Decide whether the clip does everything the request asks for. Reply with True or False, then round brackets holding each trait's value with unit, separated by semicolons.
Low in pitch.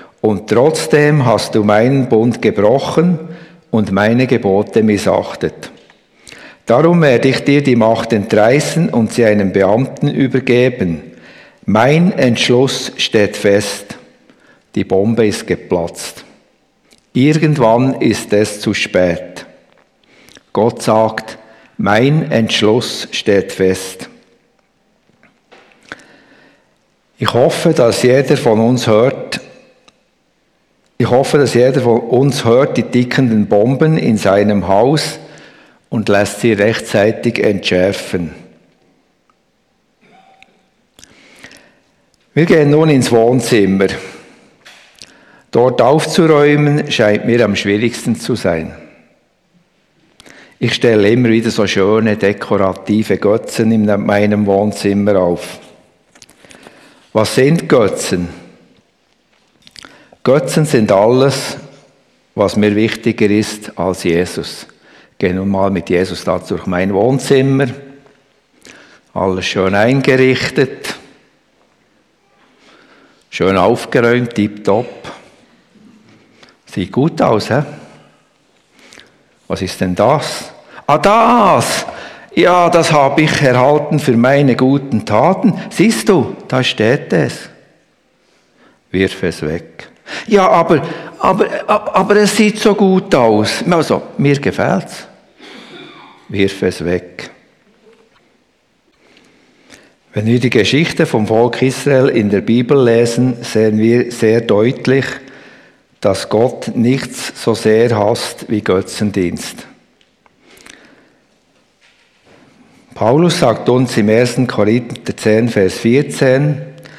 True (120 Hz)